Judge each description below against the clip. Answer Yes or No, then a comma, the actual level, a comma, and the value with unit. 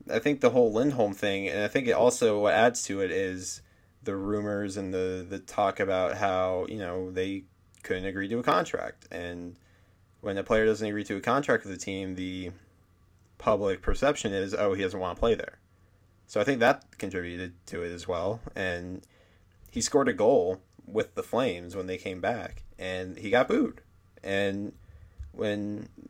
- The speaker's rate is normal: Yes, average, 185 wpm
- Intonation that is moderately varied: No, narrow, 1.8 semitones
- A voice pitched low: Yes, very low, 95 Hz